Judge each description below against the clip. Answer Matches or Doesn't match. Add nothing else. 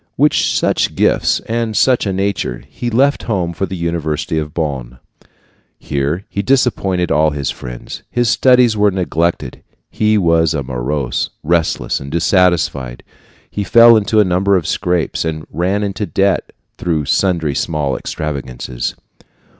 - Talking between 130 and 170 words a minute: Matches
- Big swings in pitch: Doesn't match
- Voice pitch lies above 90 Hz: Doesn't match